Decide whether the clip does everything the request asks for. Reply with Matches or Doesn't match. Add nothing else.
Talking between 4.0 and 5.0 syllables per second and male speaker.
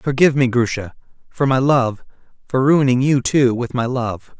Matches